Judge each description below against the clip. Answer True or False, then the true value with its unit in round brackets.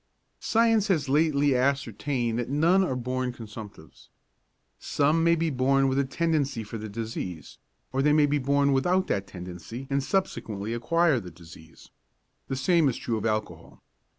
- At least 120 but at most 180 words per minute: True (160 wpm)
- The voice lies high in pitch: False (135 Hz)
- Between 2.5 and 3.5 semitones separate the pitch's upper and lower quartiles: False (5.0 semitones)